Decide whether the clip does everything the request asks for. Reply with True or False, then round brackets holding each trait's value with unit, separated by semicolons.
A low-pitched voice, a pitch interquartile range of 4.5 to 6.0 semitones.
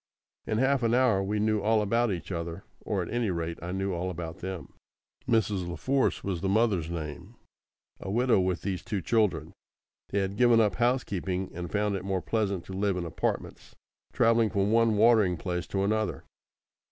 False (100 Hz; 3.7 semitones)